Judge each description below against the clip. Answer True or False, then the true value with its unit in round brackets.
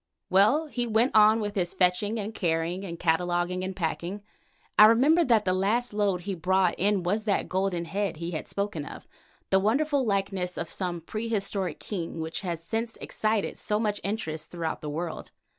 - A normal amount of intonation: True (3.6 semitones)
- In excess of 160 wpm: True (180 wpm)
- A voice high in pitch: True (195 Hz)